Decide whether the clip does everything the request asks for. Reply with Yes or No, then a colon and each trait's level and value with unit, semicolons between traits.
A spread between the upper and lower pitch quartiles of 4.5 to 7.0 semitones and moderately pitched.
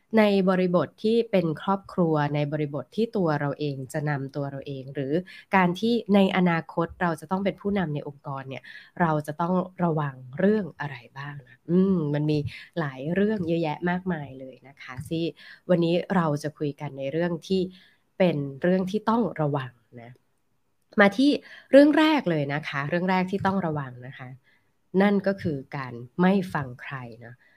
Yes: average, 4.8 semitones; medium, 165 Hz